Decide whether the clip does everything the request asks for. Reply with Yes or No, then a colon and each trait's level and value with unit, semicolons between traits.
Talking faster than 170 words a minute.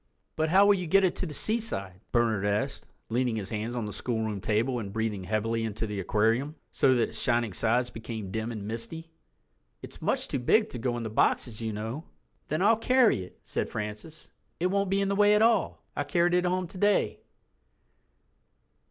Yes: average, 195 wpm